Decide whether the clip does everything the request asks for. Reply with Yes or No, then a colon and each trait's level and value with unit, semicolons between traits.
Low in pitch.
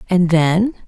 No: medium, 185 Hz